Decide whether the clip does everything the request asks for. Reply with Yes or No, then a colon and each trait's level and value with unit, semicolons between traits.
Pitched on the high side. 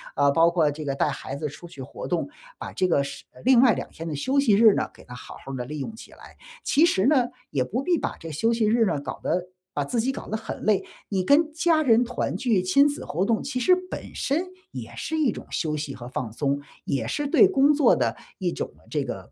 Yes: high, 200 Hz